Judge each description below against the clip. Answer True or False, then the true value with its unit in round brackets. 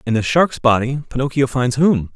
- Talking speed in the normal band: True (195 wpm)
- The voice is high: False (130 Hz)